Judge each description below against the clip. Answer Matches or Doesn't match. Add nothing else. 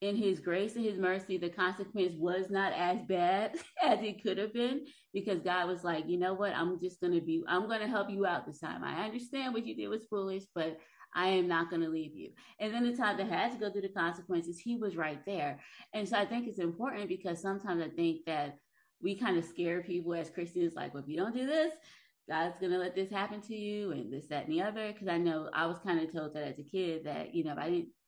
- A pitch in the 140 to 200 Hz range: Matches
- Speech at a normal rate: Doesn't match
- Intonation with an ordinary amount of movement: Matches